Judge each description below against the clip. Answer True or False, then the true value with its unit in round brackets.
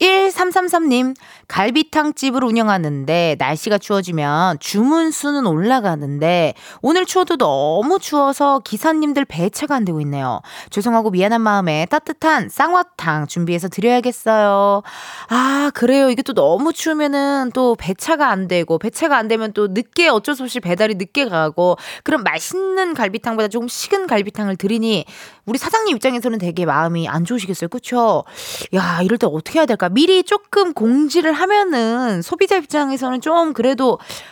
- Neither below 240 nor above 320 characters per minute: False (340 characters per minute)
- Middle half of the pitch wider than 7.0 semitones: True (7.4 semitones)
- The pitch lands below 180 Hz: False (245 Hz)